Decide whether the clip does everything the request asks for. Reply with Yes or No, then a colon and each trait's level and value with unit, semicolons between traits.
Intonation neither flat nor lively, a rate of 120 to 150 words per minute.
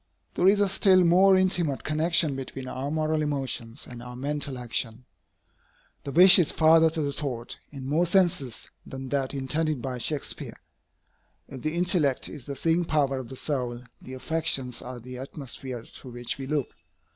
No: average, 4.0 semitones; average, 170 wpm